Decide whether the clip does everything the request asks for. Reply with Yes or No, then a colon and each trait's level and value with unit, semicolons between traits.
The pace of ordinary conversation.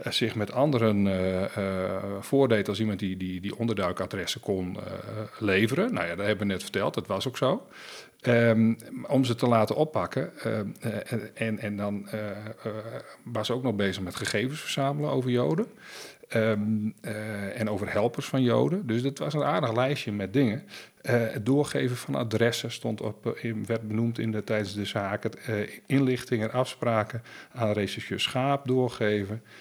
Yes: average, 170 wpm